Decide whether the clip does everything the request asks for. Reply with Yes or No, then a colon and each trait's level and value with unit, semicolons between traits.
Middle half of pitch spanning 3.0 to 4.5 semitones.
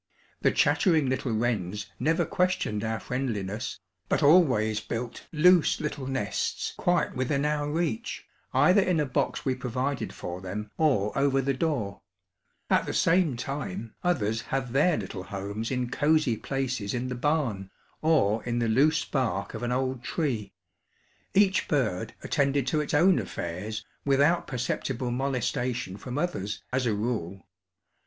No: average, 5.3 semitones